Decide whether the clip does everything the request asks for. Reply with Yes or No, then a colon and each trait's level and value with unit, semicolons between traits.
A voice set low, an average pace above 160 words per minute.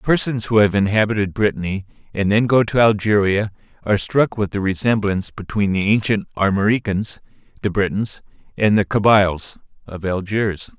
No: low, 100 Hz; average, 145 wpm